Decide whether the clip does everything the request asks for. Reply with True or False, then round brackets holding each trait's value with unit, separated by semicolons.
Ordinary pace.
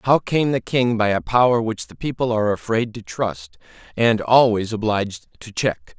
True (190 wpm)